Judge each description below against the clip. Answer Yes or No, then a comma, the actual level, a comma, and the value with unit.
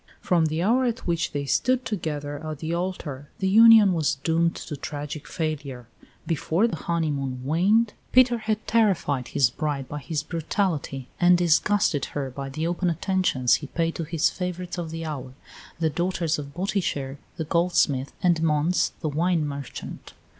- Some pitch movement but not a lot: Yes, average, 3.9 semitones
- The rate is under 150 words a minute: No, average, 165 wpm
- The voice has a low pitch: No, medium, 160 Hz